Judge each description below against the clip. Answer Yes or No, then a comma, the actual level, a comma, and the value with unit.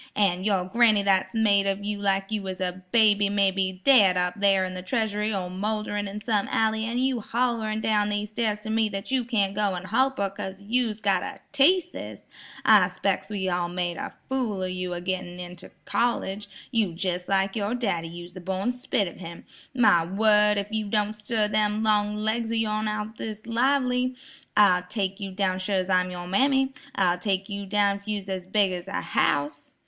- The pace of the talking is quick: Yes, fast, 210 wpm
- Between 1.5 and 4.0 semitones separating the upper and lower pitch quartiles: Yes, average, 2.7 semitones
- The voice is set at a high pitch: Yes, high, 205 Hz